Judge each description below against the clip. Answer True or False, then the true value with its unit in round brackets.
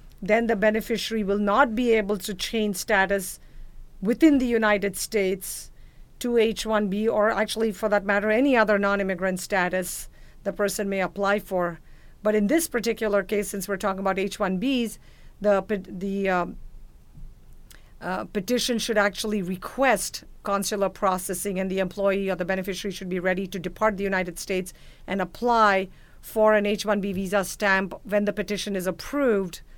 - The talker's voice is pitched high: True (200 Hz)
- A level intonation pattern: True (2.2 semitones)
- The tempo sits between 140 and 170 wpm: True (160 wpm)